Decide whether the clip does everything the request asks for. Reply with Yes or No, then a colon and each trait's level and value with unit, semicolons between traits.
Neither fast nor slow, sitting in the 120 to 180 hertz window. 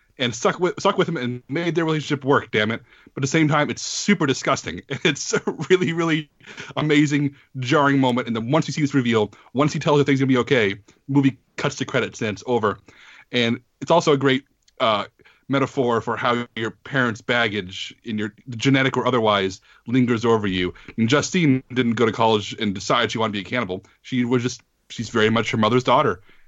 No: fast, 215 wpm; low, 130 Hz